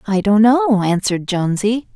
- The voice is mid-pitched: No, high, 215 Hz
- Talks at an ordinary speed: Yes, average, 155 wpm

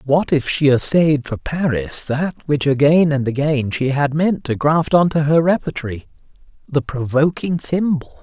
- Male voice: Yes, male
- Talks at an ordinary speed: Yes, average, 160 wpm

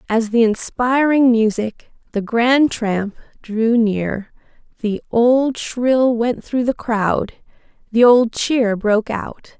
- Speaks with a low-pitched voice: No, high, 230 Hz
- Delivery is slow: Yes, slow, 130 wpm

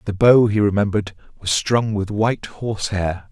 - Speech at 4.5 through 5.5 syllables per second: Yes, 5.1 syllables/s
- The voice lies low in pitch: Yes, low, 100 Hz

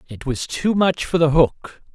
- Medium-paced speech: No, fast, 215 wpm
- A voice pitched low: No, medium, 155 Hz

